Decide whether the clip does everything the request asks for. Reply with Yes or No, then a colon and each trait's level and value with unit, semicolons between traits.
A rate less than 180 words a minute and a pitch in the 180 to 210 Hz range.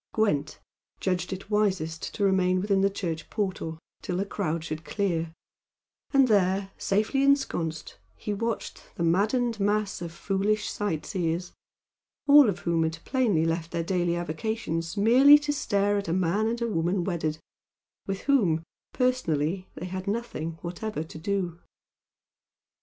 Yes: average, 145 wpm; high, 190 Hz